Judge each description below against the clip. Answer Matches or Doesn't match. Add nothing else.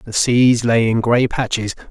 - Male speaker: Matches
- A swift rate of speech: Doesn't match